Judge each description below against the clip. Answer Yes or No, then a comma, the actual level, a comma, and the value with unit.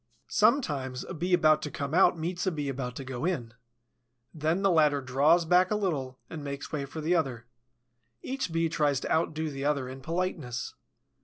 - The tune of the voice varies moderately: Yes, average, 4.0 semitones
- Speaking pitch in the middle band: Yes, medium, 155 Hz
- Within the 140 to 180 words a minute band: No, average, 190 wpm